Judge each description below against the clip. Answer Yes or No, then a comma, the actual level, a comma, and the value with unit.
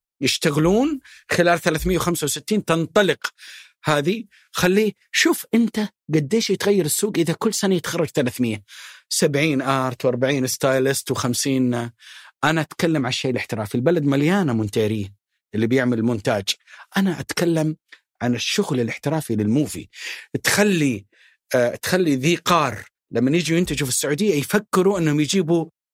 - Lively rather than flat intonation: Yes, wide, 6.0 semitones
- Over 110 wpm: Yes, average, 120 wpm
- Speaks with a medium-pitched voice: Yes, medium, 155 Hz